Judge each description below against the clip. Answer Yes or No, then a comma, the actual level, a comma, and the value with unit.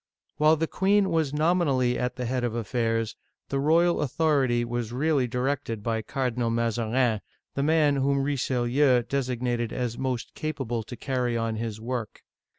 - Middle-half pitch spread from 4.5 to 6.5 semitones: No, average, 3.4 semitones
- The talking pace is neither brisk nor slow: Yes, average, 155 wpm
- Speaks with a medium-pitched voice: No, low, 125 Hz